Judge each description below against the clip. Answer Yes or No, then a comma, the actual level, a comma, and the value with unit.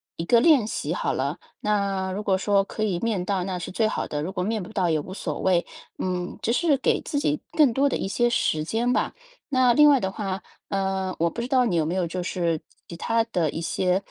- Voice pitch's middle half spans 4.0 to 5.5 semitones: Yes, average, 4.5 semitones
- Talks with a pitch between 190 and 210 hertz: Yes, high, 195 Hz